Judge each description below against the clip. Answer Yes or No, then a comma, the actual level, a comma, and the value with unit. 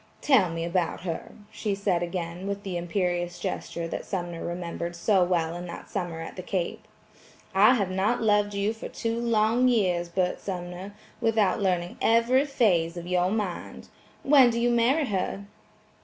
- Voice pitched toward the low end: No, high, 190 Hz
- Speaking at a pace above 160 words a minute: Yes, average, 170 wpm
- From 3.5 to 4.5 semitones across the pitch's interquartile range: Yes, average, 3.9 semitones